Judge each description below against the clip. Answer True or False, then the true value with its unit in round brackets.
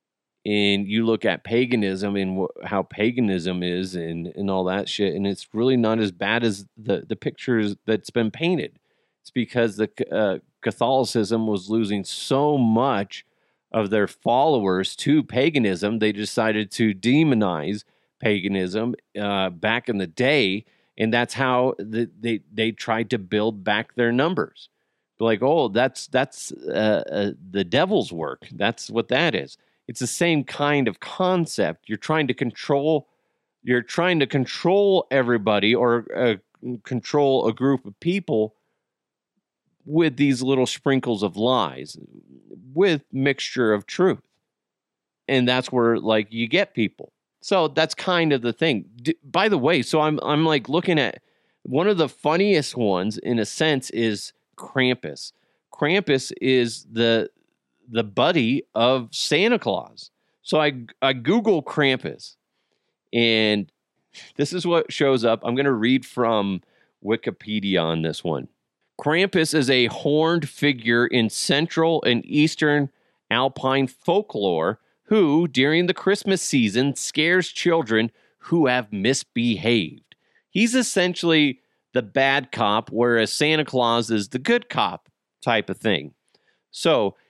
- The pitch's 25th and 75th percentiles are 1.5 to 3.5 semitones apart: False (5.2 semitones)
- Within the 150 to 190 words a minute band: False (140 wpm)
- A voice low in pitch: True (125 Hz)